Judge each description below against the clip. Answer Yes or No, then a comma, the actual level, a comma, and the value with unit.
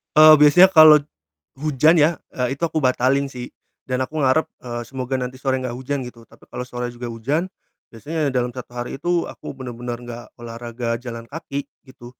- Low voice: Yes, low, 130 Hz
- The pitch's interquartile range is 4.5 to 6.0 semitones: No, average, 3.3 semitones